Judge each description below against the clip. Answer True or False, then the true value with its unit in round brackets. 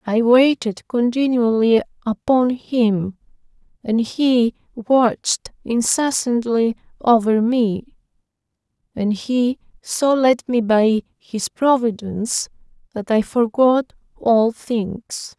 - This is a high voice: True (235 Hz)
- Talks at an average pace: False (95 wpm)